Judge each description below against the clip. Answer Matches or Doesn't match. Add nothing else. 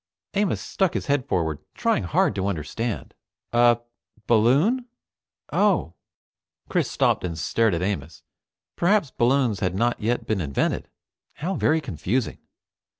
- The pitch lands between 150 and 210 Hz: Doesn't match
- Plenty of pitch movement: Matches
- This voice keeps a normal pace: Doesn't match